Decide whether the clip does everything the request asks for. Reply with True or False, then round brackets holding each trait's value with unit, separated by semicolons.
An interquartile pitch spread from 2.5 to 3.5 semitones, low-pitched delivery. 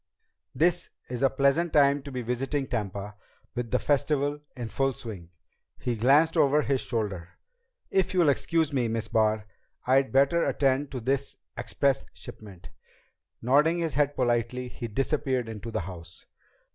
False (4.0 semitones; 130 Hz)